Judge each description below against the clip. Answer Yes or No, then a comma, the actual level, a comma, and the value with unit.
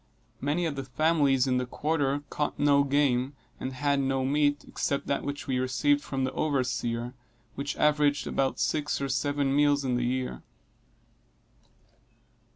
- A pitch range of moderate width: No, narrow, 1.9 semitones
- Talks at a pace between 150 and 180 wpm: Yes, average, 155 wpm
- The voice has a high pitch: No, medium, 140 Hz